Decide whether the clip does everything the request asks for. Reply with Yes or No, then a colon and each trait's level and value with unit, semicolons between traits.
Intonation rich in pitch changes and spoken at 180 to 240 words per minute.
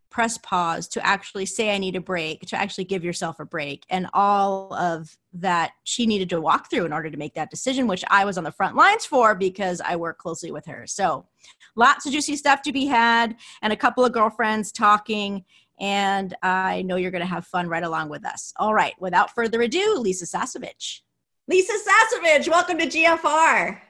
Yes: wide, 5.7 semitones; fast, 205 wpm